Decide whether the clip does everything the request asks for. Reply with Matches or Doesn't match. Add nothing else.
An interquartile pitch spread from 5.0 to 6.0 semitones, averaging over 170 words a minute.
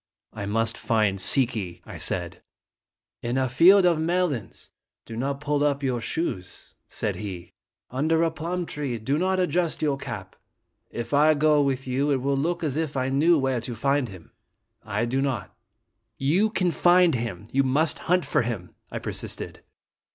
Matches